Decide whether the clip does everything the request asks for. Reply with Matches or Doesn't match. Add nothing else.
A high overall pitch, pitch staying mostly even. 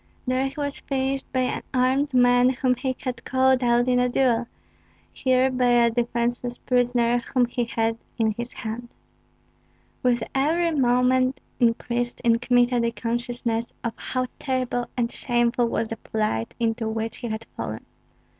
Matches